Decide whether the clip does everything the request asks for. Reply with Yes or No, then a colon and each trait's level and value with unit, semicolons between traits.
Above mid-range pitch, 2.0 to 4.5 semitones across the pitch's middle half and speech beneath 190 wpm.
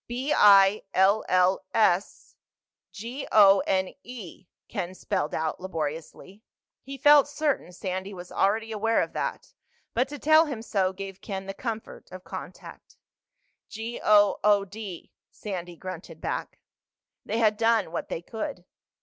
Yes: high, 200 Hz; average, 3.4 semitones; average, 145 wpm